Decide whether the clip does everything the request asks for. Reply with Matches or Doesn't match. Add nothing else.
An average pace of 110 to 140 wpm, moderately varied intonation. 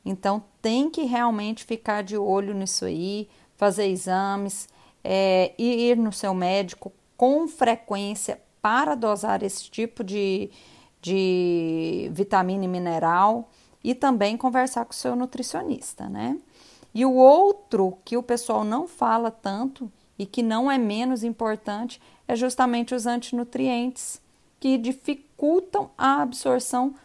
Matches